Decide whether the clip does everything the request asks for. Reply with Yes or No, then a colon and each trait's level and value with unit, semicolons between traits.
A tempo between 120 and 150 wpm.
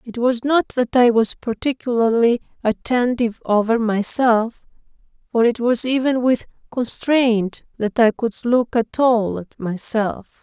Yes: average, 140 wpm